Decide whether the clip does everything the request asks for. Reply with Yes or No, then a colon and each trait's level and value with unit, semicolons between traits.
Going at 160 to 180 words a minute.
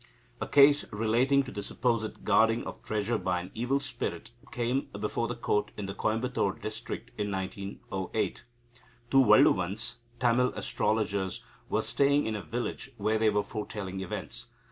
No: average, 150 wpm